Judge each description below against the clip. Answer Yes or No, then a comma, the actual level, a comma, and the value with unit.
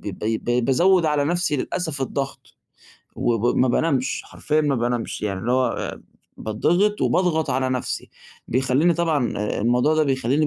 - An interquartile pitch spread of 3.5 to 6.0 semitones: Yes, average, 4.4 semitones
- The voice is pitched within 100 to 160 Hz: Yes, low, 135 Hz